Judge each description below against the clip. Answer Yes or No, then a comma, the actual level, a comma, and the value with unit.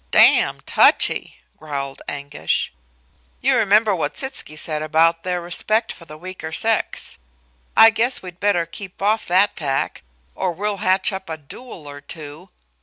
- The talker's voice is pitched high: No, medium, 180 Hz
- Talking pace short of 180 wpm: Yes, average, 150 wpm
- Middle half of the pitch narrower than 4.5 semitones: No, average, 5.0 semitones